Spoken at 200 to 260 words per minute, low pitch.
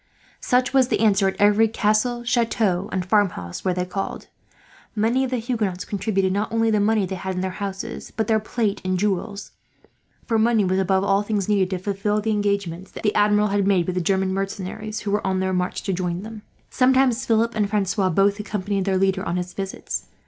No: fast, 205 wpm; high, 200 Hz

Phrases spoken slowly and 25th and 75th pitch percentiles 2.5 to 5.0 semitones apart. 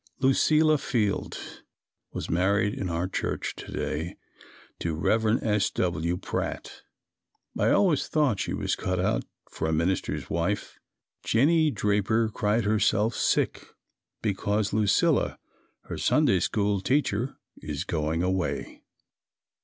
Yes: slow, 120 wpm; average, 4.0 semitones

